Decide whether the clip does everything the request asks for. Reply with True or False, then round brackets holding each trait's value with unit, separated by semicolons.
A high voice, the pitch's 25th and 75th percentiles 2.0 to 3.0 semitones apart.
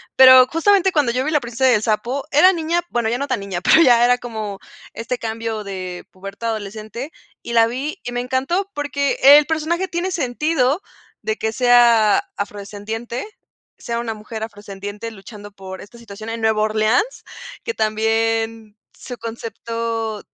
False (230 Hz; 3.6 semitones)